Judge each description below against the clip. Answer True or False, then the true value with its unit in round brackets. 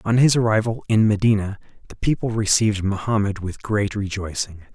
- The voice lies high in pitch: False (105 Hz)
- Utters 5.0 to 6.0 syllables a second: True (5.5 syllables/s)